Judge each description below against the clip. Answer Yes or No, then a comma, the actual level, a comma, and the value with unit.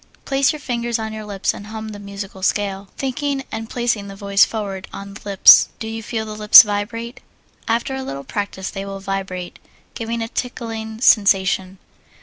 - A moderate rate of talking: Yes, average, 180 wpm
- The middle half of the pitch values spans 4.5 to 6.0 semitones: No, average, 2.7 semitones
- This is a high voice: Yes, high, 215 Hz